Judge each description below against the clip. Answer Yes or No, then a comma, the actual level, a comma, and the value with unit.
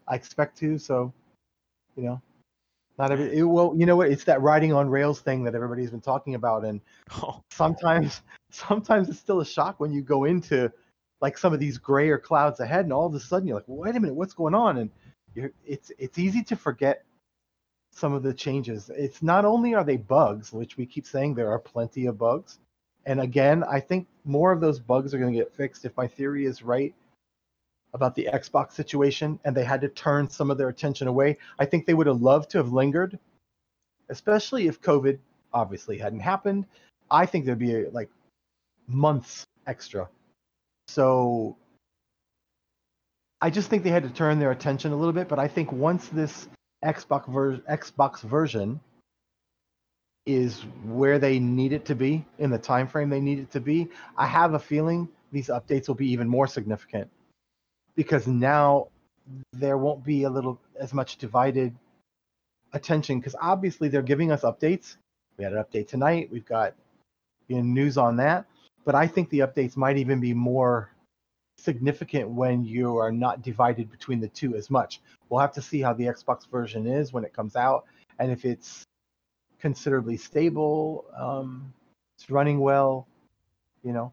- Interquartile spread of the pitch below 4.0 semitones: Yes, average, 3.5 semitones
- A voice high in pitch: No, medium, 140 Hz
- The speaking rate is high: No, average, 185 wpm